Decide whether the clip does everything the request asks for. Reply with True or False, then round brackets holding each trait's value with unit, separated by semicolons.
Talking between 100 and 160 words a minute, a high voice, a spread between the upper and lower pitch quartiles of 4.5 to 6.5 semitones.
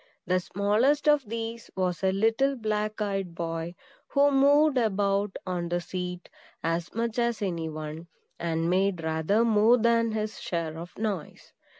True (155 wpm; 200 Hz; 4.9 semitones)